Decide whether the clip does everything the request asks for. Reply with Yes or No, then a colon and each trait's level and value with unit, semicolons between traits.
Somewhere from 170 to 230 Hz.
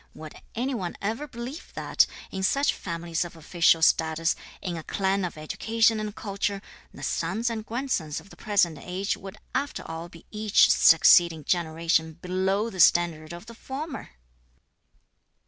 Yes: medium, 185 Hz